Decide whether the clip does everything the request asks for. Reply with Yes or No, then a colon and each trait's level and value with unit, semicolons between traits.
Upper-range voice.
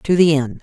No: medium, 155 Hz